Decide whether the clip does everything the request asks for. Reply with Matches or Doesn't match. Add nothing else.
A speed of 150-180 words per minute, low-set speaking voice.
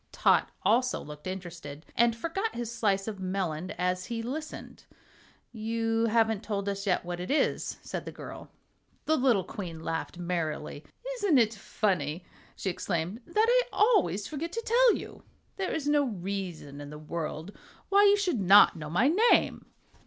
Doesn't match